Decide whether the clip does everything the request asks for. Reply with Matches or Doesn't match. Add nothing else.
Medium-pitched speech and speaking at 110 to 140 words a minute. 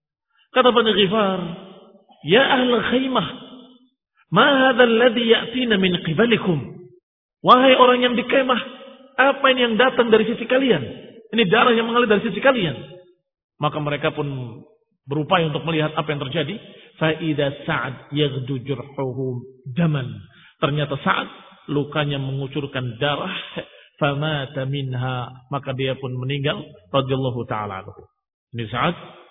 Matches